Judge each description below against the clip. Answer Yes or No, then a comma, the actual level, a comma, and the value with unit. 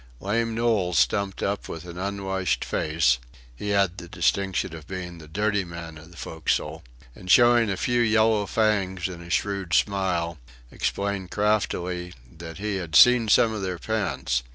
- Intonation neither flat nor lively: Yes, average, 3.4 semitones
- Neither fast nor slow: Yes, average, 165 wpm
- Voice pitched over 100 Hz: No, very low, 95 Hz